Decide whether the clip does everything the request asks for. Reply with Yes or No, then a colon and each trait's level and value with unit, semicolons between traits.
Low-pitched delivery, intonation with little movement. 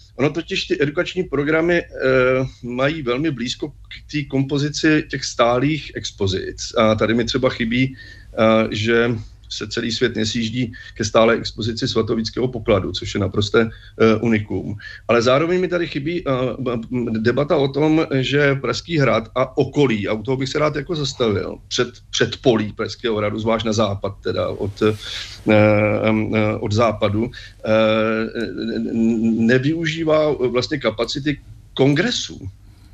No: low, 120 Hz; average, 4.1 semitones